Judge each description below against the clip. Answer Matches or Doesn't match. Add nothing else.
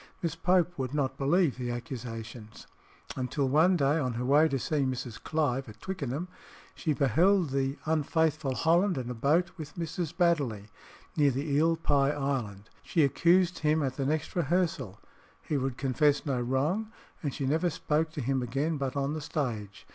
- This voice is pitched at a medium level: Matches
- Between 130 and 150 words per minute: Doesn't match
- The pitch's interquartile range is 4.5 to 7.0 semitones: Doesn't match